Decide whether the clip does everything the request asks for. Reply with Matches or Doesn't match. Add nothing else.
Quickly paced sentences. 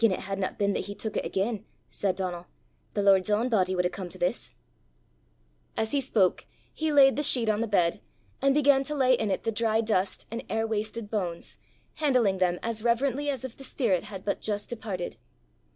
Matches